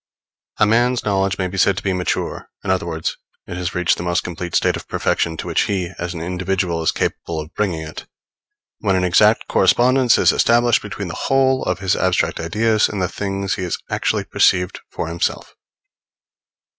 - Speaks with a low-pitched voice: Yes, very low, 95 Hz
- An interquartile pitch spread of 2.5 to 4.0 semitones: Yes, average, 2.9 semitones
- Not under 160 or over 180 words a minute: No, average, 195 wpm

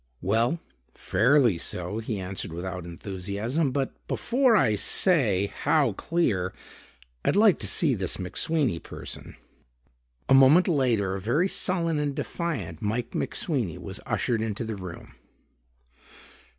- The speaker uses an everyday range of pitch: No, wide, 8.1 semitones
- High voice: No, low, 115 Hz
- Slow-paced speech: Yes, slow, 125 wpm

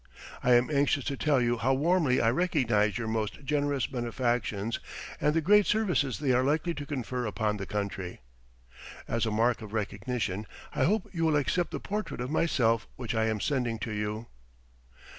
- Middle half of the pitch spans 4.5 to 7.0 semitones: Yes, average, 4.9 semitones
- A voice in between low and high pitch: No, low, 125 Hz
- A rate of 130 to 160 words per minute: No, average, 180 wpm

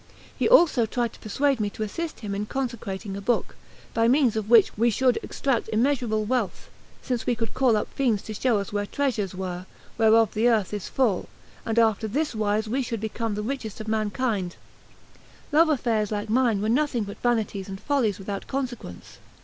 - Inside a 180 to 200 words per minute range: Yes, average, 190 wpm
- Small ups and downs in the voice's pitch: No, average, 3.3 semitones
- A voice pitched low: No, high, 225 Hz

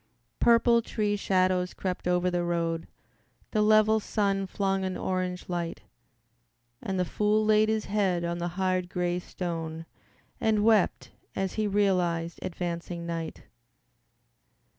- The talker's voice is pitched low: No, medium, 185 Hz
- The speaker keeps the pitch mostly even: No, average, 3.1 semitones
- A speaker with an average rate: No, slow, 130 wpm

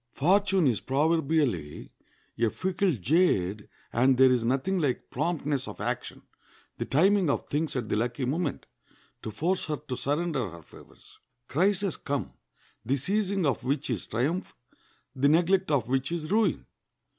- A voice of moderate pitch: Yes, medium, 145 Hz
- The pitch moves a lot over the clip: Yes, wide, 5.8 semitones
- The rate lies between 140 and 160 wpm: Yes, average, 150 wpm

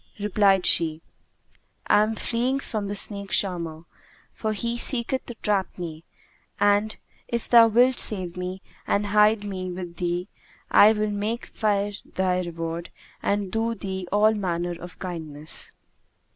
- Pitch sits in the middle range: No, high, 200 Hz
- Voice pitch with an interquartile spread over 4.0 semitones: No, average, 3.3 semitones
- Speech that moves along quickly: No, average, 145 wpm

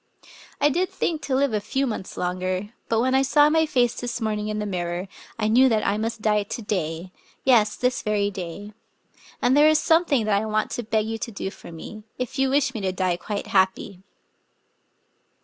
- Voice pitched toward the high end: Yes, high, 215 Hz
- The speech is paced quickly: Yes, fast, 220 wpm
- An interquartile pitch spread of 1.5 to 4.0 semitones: No, average, 4.5 semitones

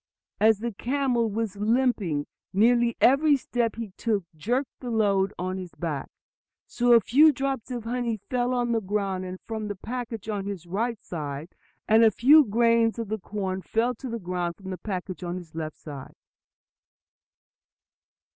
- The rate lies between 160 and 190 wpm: Yes, average, 170 wpm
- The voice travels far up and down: No, average, 4.2 semitones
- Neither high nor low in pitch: No, high, 220 Hz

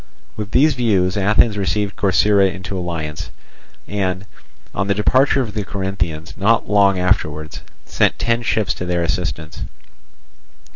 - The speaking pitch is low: Yes, low, 100 Hz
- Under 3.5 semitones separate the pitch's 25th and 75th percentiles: Yes, average, 2.8 semitones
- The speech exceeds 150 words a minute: No, slow, 135 wpm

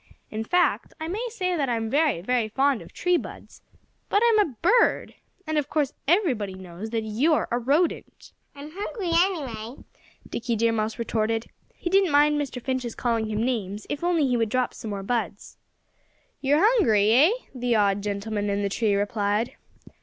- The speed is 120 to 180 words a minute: Yes, average, 175 wpm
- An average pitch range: No, wide, 6.3 semitones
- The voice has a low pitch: No, high, 245 Hz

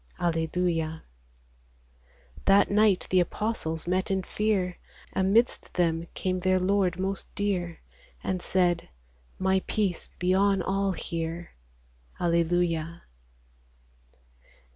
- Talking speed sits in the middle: No, slow, 100 wpm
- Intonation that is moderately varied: No, narrow, 2.3 semitones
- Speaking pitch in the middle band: Yes, medium, 180 Hz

